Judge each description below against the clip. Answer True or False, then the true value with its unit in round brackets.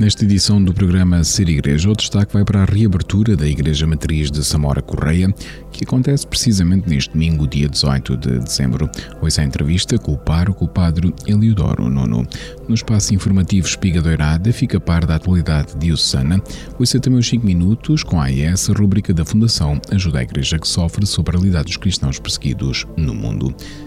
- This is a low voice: True (90 Hz)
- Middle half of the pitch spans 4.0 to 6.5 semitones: True (5.1 semitones)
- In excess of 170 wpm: True (185 wpm)